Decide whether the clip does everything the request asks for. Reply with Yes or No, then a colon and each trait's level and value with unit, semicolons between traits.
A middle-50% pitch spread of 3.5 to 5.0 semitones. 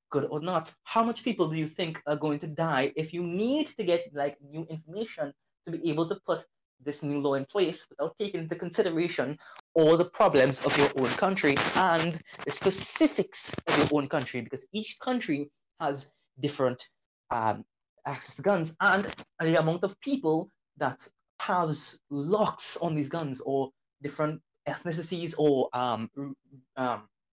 Yes: average, 3.9 semitones